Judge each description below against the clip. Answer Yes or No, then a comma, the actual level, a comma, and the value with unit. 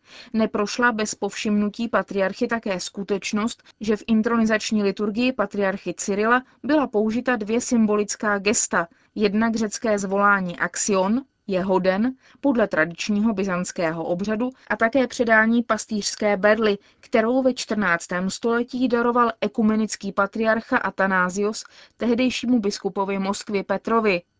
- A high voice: Yes, high, 215 Hz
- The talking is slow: Yes, slow, 110 wpm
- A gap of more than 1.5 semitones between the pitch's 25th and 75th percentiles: Yes, average, 2.9 semitones